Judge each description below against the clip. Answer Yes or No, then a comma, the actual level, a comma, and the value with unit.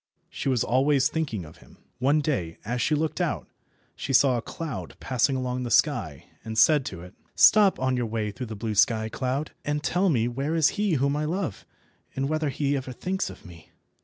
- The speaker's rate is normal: No, fast, 210 wpm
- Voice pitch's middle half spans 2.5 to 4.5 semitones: No, average, 5.0 semitones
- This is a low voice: Yes, low, 130 Hz